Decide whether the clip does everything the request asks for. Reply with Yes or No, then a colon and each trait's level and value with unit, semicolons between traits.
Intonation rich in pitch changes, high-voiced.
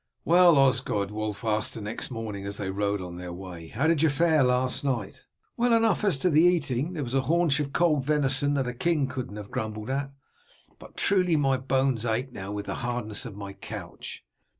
No: wide, 5.9 semitones; low, 130 Hz